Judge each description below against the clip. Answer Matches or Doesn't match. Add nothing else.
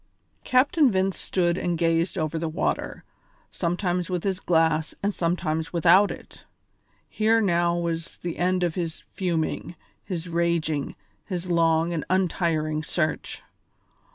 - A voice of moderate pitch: Matches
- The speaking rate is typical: Doesn't match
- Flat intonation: Matches